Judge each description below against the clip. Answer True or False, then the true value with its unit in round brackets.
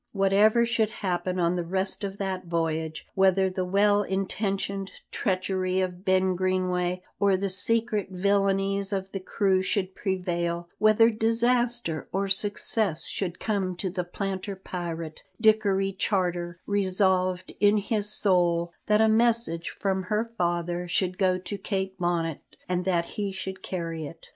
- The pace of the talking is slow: False (145 wpm)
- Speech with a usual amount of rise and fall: False (2.0 semitones)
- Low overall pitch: False (190 Hz)